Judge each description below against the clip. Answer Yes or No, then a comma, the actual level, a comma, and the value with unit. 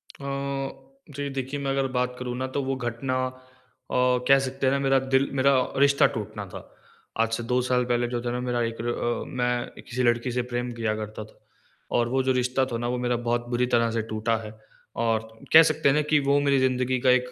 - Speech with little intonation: Yes, narrow, 2.1 semitones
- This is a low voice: Yes, low, 125 Hz